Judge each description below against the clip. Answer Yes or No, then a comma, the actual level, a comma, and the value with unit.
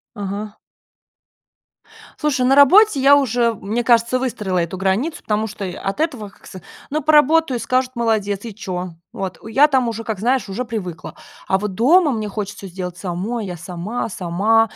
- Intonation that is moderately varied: Yes, average, 4.8 semitones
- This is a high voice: Yes, high, 220 Hz